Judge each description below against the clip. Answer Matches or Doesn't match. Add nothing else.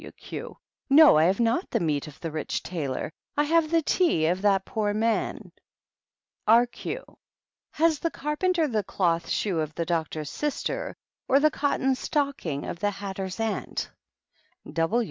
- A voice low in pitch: Doesn't match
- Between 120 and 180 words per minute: Matches